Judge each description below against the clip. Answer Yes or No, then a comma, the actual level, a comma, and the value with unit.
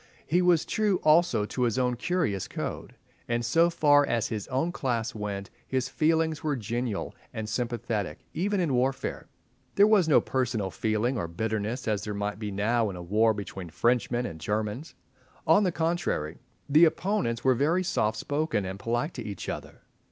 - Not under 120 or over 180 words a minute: Yes, average, 175 wpm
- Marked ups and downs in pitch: Yes, wide, 6.6 semitones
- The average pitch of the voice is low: Yes, low, 120 Hz